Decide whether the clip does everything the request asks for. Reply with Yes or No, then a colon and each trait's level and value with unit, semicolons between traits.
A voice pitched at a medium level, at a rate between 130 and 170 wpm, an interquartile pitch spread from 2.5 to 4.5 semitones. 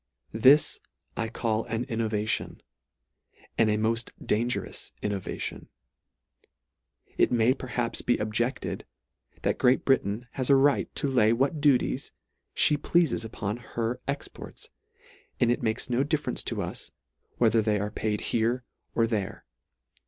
No: low, 115 Hz; average, 140 wpm; average, 2.9 semitones